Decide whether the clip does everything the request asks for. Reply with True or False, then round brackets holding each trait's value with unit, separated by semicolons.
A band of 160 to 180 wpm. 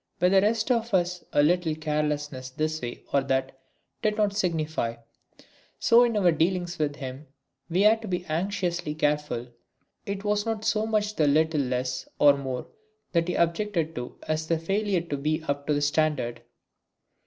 True (175 wpm)